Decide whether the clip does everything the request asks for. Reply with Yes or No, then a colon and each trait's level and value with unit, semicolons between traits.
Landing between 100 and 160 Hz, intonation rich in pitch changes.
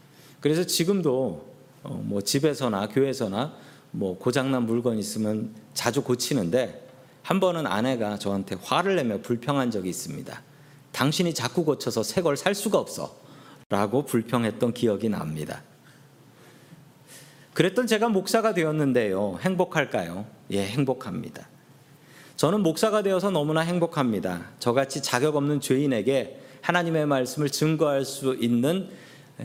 No: medium, 140 Hz; average, 4.7 semitones